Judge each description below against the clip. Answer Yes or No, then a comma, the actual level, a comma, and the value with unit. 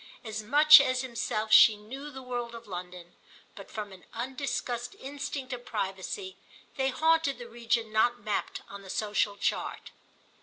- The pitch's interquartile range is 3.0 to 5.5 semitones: Yes, average, 4.0 semitones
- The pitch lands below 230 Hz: No, high, 235 Hz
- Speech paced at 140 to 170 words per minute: Yes, average, 155 wpm